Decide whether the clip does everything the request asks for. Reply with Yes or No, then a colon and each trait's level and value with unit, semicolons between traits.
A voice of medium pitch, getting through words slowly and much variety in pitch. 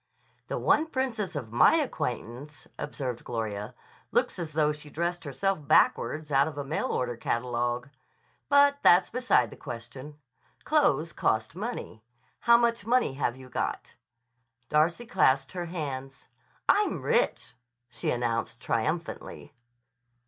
Yes: medium, 150 Hz; slow, 130 wpm; wide, 7.8 semitones